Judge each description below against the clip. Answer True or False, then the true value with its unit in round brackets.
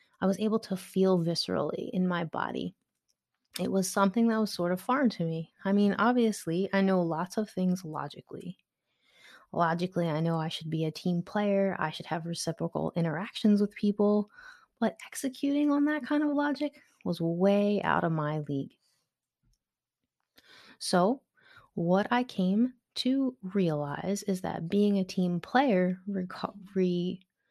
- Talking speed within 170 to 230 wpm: False (155 wpm)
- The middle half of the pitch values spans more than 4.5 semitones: False (4.1 semitones)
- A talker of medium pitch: False (195 Hz)